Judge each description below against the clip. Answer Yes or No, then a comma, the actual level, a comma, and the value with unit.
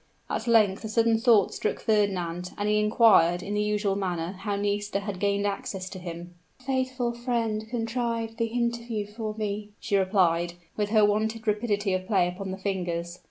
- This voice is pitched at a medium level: No, high, 205 Hz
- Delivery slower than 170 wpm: No, average, 180 wpm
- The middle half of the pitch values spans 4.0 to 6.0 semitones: No, average, 3.0 semitones